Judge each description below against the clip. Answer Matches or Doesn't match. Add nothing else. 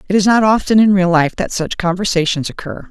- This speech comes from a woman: Matches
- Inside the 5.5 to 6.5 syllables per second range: Matches